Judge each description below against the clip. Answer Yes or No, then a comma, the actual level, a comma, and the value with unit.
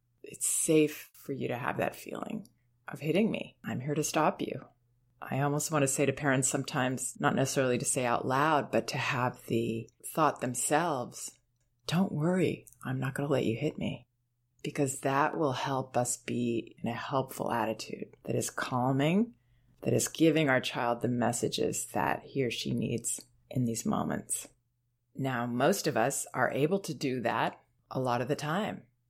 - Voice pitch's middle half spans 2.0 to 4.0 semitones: Yes, average, 3.7 semitones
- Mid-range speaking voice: No, low, 130 Hz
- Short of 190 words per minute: Yes, average, 180 wpm